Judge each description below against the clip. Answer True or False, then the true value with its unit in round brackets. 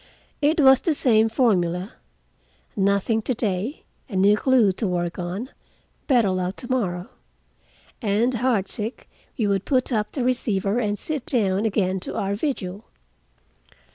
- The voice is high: True (210 Hz)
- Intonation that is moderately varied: True (4.5 semitones)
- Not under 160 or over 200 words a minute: False (140 wpm)